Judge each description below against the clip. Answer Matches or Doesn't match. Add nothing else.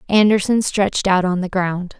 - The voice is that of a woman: Matches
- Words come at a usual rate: Matches